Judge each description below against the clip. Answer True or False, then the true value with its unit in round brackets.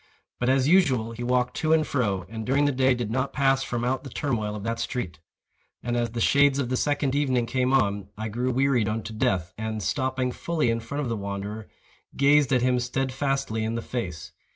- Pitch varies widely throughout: False (3.4 semitones)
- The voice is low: True (125 Hz)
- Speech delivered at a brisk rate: True (215 wpm)